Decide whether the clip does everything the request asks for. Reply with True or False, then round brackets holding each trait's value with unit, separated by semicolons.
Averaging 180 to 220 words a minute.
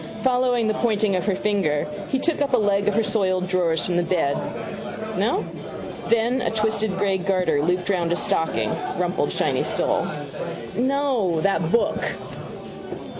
False (155 wpm)